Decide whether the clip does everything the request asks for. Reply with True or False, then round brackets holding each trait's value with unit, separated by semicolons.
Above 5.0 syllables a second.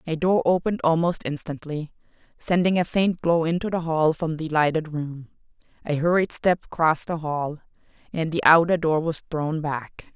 False (4.8 syllables/s)